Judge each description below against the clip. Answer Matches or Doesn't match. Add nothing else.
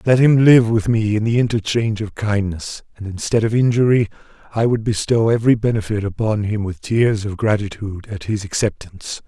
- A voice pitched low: Matches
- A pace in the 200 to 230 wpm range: Doesn't match